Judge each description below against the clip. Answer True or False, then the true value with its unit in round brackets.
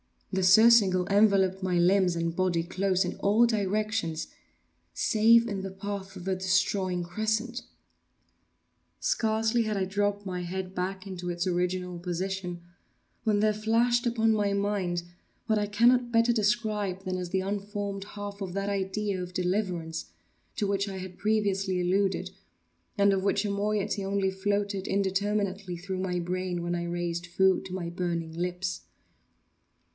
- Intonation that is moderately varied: False (2.2 semitones)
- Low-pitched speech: False (195 Hz)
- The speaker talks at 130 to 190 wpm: True (150 wpm)